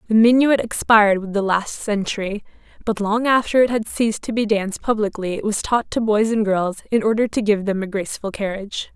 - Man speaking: No, female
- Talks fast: Yes, fast, 215 wpm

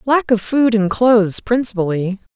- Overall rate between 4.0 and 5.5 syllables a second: Yes, 4.7 syllables/s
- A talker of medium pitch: No, high, 220 Hz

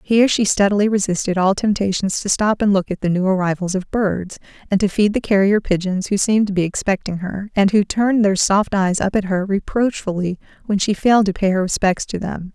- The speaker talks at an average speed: No, fast, 225 wpm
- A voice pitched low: No, high, 195 Hz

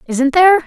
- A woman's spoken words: Yes, female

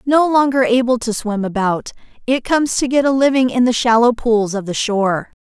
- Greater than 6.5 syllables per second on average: No, 5.3 syllables/s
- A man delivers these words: No, female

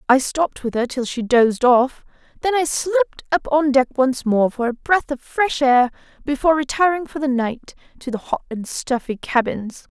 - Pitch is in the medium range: No, very high, 270 Hz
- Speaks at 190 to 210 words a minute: Yes, average, 200 wpm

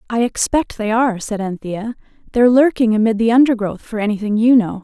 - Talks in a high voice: Yes, high, 225 Hz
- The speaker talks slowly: No, average, 185 wpm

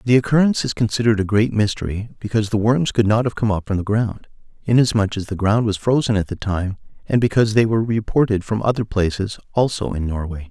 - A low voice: Yes, low, 110 Hz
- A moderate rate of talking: No, fast, 215 wpm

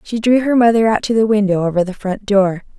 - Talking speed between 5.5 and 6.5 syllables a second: Yes, 5.8 syllables/s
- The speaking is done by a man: No, female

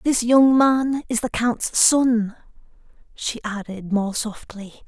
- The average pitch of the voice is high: Yes, high, 235 Hz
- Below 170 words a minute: Yes, slow, 135 wpm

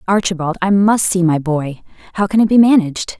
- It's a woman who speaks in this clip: Yes, female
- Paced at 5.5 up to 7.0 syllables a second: Yes, 5.7 syllables/s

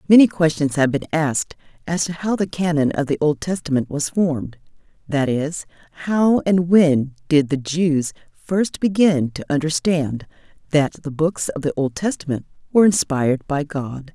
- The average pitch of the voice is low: No, medium, 155 Hz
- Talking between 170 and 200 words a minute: No, average, 160 wpm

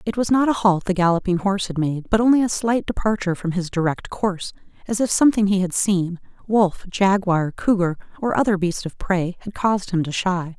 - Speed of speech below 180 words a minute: No, fast, 205 wpm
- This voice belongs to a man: No, female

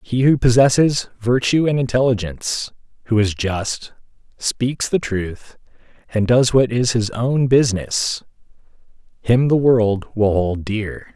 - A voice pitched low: Yes, low, 115 Hz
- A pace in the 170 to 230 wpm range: No, slow, 135 wpm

